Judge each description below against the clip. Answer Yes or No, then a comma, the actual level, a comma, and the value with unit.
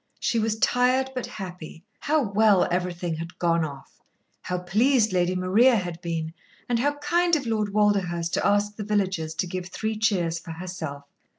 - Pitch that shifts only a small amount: No, average, 4.4 semitones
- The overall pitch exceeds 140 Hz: Yes, high, 190 Hz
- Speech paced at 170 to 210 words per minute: Yes, average, 175 wpm